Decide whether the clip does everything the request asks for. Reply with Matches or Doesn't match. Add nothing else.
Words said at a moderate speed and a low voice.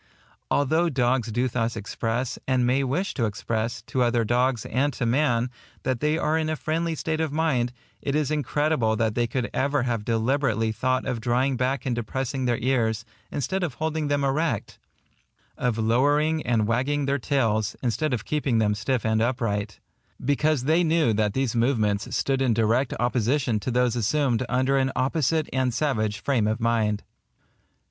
Matches